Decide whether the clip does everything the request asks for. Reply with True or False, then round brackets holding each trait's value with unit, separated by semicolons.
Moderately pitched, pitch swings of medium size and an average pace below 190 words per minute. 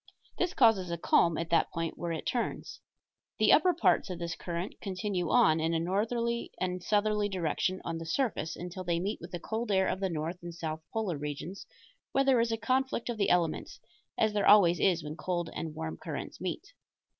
False (180 Hz; 4.2 semitones; 205 wpm)